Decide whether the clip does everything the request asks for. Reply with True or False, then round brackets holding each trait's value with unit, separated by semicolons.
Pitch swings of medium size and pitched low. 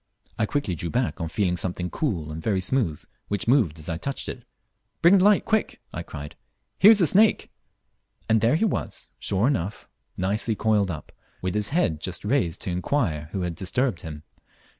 False (7.7 semitones; 100 Hz)